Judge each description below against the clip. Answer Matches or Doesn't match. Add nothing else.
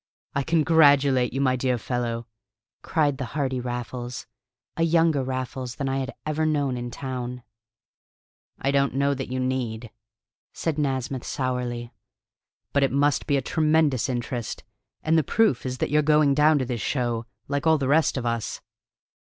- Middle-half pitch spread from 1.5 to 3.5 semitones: Matches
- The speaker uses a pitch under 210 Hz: Matches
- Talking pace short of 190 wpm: Matches